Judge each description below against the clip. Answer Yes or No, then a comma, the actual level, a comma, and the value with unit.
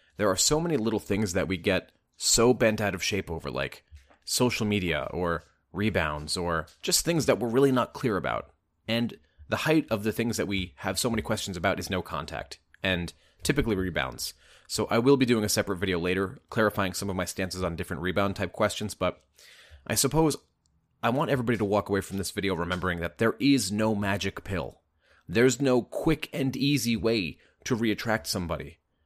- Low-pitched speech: Yes, low, 100 Hz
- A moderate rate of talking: Yes, average, 195 wpm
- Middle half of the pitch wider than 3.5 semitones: Yes, average, 4.2 semitones